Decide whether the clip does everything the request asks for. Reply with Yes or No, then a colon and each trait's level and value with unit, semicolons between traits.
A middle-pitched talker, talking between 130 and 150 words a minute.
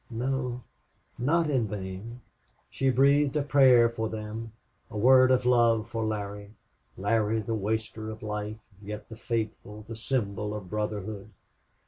No: low, 110 Hz; average, 140 wpm